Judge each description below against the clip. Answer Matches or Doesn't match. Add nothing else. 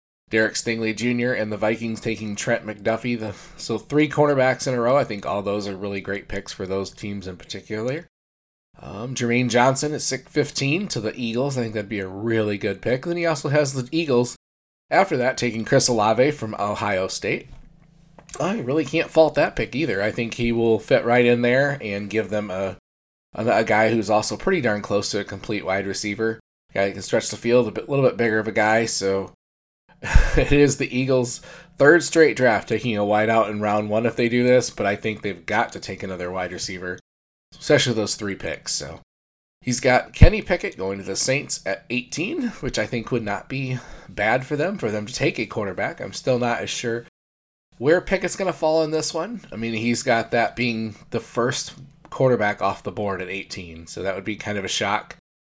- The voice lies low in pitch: Matches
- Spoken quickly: Matches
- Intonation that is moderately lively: Matches